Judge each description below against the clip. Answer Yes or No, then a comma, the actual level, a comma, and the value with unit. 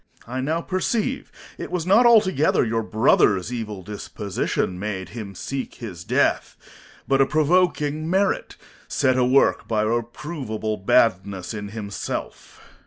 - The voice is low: Yes, low, 120 Hz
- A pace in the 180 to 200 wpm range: No, slow, 135 wpm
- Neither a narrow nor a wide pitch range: No, wide, 6.8 semitones